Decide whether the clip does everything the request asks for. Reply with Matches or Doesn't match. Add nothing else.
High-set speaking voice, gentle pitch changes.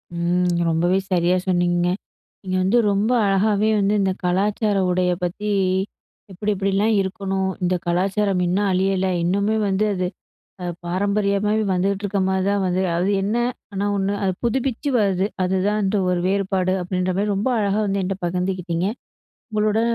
Matches